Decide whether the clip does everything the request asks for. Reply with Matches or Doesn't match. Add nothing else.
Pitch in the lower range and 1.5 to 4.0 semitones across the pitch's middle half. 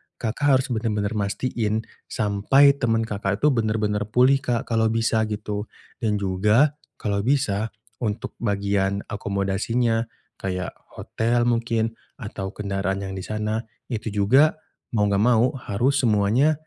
Matches